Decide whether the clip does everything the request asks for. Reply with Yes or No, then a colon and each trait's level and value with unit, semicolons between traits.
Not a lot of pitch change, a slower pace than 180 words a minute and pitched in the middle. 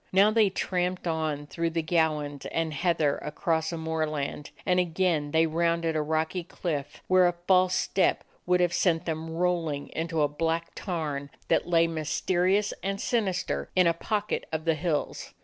Yes: narrow, 2.3 semitones; average, 165 wpm; medium, 165 Hz